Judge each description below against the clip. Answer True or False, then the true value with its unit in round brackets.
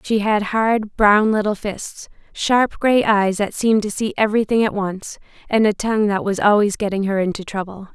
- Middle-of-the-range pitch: False (210 Hz)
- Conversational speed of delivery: True (195 wpm)